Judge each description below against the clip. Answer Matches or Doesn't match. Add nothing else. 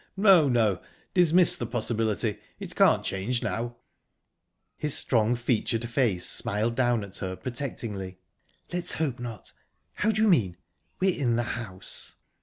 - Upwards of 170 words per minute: Doesn't match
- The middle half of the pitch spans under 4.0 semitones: Doesn't match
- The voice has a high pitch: Doesn't match